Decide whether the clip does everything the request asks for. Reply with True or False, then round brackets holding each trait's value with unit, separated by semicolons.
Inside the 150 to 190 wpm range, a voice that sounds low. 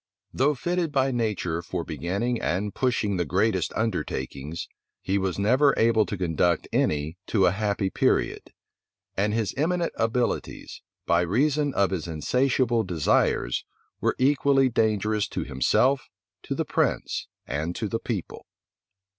False (140 wpm; 105 Hz)